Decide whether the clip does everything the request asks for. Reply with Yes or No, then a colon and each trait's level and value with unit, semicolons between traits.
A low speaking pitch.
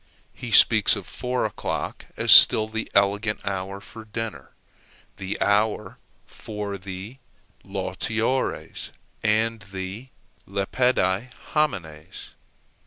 Yes: low, 105 Hz